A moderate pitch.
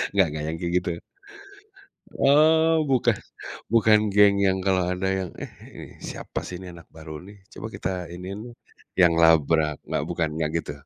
No: very low, 90 Hz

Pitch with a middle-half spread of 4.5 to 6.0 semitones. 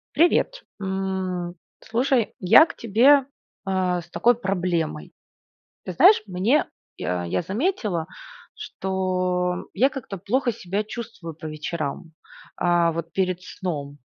Yes: average, 4.9 semitones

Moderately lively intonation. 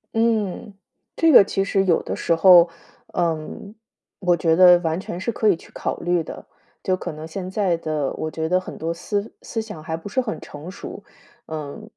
Yes: average, 3.7 semitones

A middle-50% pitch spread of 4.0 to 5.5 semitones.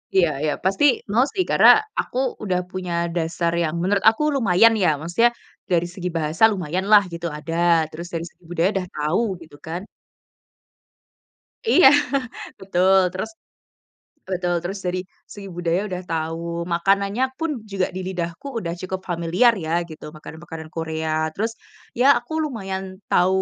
No: average, 2.9 semitones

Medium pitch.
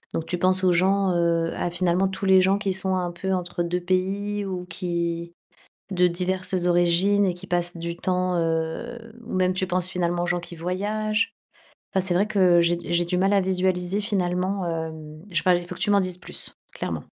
Yes: medium, 180 Hz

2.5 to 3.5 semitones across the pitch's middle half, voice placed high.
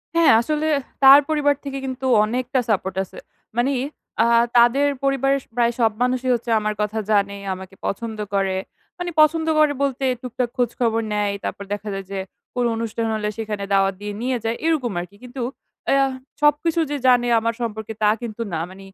No: average, 4.4 semitones; high, 235 Hz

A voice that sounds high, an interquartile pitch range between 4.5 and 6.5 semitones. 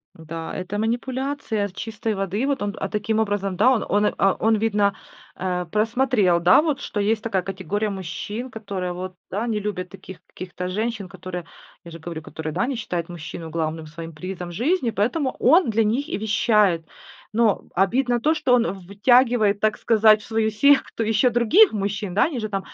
No: high, 210 Hz; average, 3.9 semitones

